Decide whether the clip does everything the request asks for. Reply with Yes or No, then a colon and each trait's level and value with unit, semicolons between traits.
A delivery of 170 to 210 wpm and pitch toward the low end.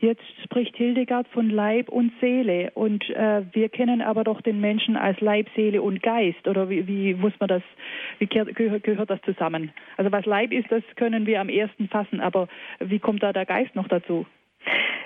No: fast, 190 wpm; high, 215 Hz